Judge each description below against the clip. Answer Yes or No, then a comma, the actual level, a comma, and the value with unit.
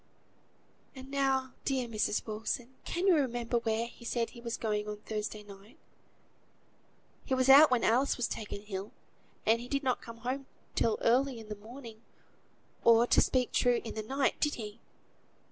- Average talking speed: Yes, average, 175 wpm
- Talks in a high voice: Yes, high, 235 Hz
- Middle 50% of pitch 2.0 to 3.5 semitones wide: Yes, average, 3.1 semitones